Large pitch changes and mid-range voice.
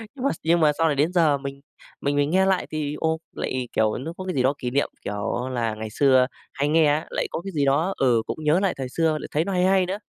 No: average, 4.1 semitones; medium, 150 Hz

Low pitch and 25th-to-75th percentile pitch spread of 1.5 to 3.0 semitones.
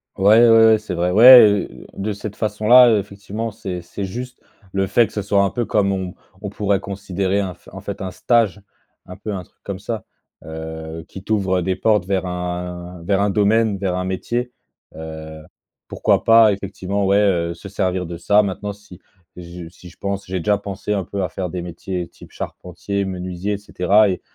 Yes: low, 100 Hz; narrow, 2.5 semitones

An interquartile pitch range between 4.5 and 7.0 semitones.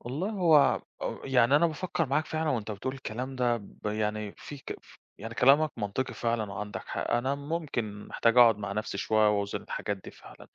Yes: average, 5.1 semitones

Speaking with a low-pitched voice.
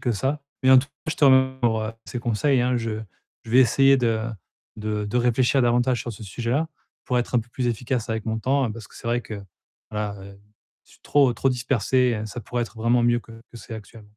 Yes: low, 120 Hz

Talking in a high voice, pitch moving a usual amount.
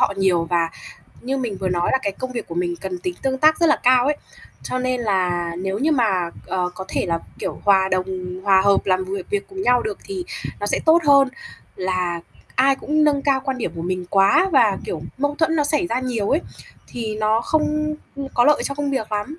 No: high, 220 Hz; wide, 7.0 semitones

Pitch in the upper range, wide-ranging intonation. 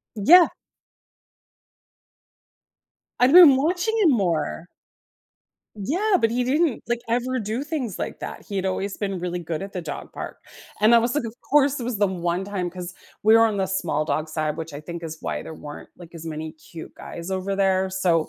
Yes: high, 195 Hz; wide, 6.4 semitones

